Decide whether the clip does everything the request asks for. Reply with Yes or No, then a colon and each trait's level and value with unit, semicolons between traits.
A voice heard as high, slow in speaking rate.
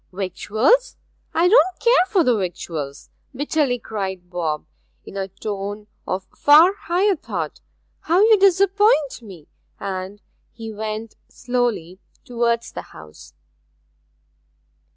Yes: high, 225 Hz; slow, 110 wpm